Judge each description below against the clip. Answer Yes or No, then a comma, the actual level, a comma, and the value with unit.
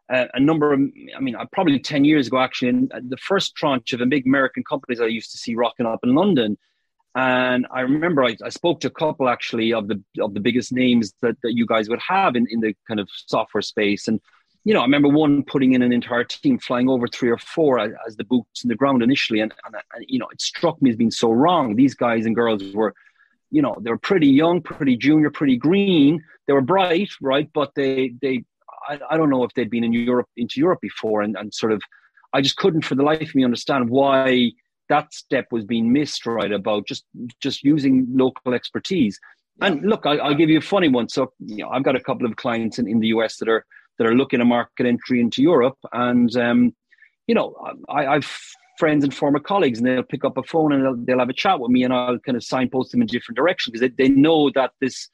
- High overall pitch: No, low, 130 Hz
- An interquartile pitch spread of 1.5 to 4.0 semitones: No, average, 4.4 semitones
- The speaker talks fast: Yes, fast, 240 wpm